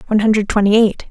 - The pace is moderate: No, fast, 215 wpm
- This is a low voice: No, high, 210 Hz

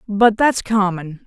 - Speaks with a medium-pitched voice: No, high, 205 Hz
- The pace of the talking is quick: No, average, 140 wpm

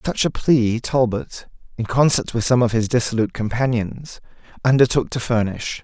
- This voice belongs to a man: Yes, male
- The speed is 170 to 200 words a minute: No, average, 155 wpm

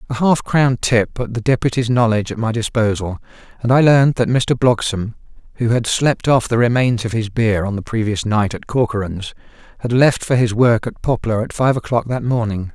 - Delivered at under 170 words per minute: No, fast, 205 wpm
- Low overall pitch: Yes, low, 115 Hz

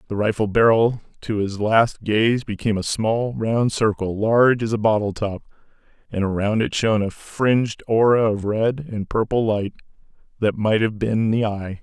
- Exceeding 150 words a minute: Yes, average, 180 wpm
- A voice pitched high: No, low, 110 Hz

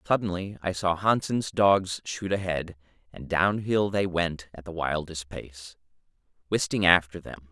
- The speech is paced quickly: No, average, 145 wpm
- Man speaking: Yes, male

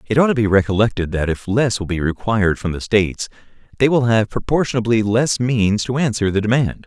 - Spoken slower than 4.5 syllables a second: No, 5.8 syllables/s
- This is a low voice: Yes, low, 110 Hz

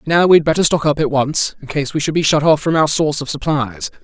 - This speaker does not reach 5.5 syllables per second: No, 6.1 syllables/s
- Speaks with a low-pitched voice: No, medium, 150 Hz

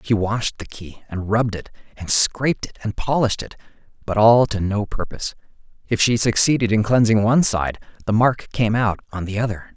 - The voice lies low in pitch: Yes, low, 110 Hz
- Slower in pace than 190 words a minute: No, average, 195 wpm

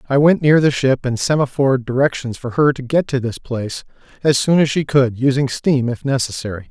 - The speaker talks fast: Yes, fast, 215 wpm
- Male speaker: Yes, male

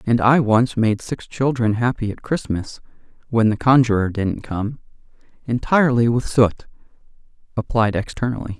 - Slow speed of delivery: Yes, slow, 125 wpm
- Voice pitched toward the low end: Yes, low, 115 Hz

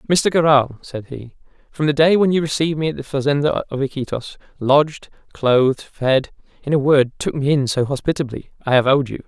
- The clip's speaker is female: No, male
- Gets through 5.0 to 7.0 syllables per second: Yes, 5.6 syllables/s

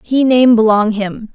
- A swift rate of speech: No, average, 180 wpm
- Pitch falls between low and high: No, high, 225 Hz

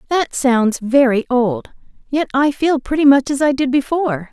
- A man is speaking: No, female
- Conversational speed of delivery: Yes, average, 180 wpm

